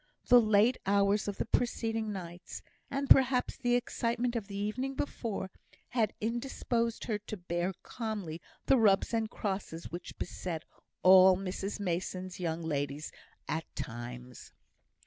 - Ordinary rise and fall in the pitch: Yes, average, 4.7 semitones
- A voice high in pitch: Yes, high, 200 Hz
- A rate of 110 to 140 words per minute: Yes, slow, 135 wpm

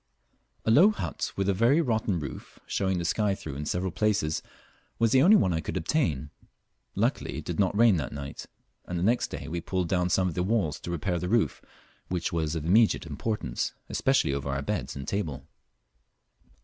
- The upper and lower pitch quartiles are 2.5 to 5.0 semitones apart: No, wide, 5.4 semitones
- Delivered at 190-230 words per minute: Yes, average, 200 wpm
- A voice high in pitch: No, very low, 90 Hz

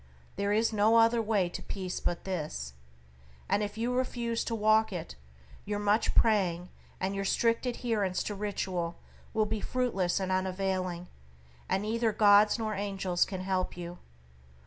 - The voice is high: Yes, high, 205 Hz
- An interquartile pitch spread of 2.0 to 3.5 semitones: Yes, average, 3.0 semitones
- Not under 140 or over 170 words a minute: Yes, average, 155 wpm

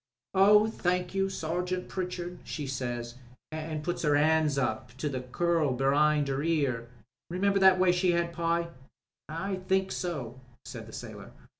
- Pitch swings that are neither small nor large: Yes, average, 4.2 semitones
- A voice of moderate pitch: Yes, medium, 165 Hz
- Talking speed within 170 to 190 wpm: No, average, 155 wpm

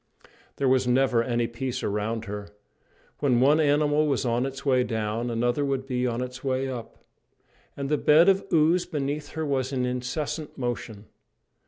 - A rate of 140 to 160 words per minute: No, average, 170 wpm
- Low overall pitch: Yes, low, 130 Hz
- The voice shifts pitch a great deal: No, average, 3.2 semitones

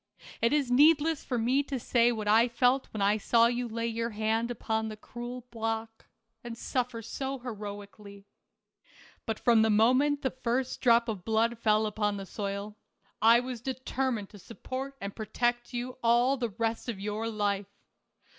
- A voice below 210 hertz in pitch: No, high, 230 Hz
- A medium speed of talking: Yes, average, 170 wpm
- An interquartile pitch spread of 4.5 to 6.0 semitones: No, narrow, 2.5 semitones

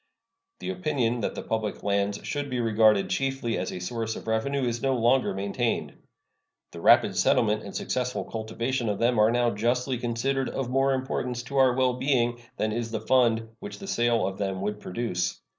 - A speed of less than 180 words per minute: No, average, 190 wpm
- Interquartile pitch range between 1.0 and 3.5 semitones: Yes, average, 2.9 semitones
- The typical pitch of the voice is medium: No, low, 120 Hz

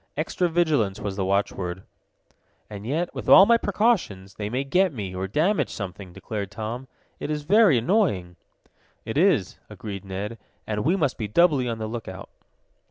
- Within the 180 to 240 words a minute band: No, average, 165 wpm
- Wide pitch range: Yes, wide, 8.7 semitones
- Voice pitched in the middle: No, low, 115 Hz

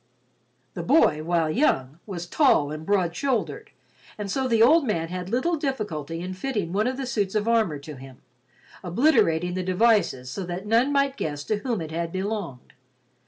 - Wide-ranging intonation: Yes, wide, 6.2 semitones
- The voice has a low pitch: No, high, 190 Hz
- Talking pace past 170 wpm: Yes, average, 180 wpm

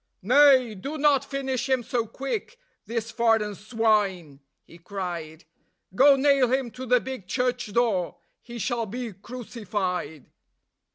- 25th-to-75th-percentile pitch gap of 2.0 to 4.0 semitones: No, average, 4.5 semitones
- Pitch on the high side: Yes, high, 235 Hz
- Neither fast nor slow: No, slow, 130 wpm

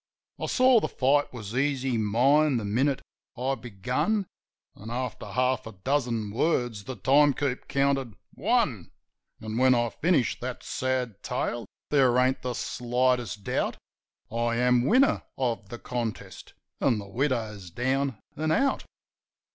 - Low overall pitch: Yes, low, 125 Hz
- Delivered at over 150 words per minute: No, average, 140 wpm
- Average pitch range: Yes, average, 3.0 semitones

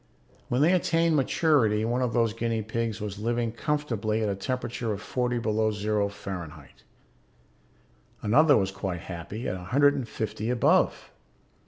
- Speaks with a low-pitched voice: Yes, low, 115 Hz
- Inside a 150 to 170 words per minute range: Yes, average, 155 wpm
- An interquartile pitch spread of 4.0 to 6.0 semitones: No, average, 3.3 semitones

